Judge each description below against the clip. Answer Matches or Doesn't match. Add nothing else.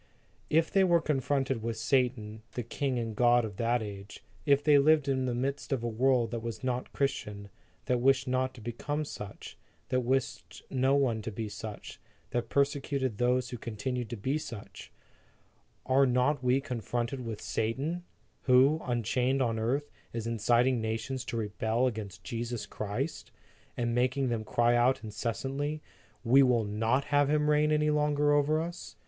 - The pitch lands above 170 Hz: Doesn't match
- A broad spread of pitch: Doesn't match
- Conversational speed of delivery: Matches